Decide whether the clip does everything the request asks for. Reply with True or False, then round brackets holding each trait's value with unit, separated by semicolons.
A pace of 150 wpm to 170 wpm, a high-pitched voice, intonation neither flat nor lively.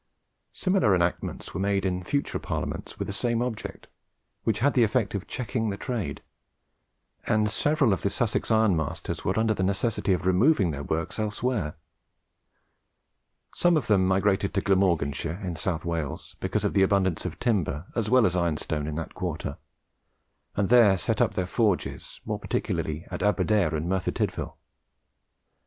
False (165 wpm; 100 Hz; 4.2 semitones)